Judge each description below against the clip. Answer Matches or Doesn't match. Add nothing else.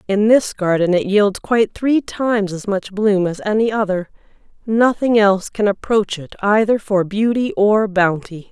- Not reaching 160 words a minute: Doesn't match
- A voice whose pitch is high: Matches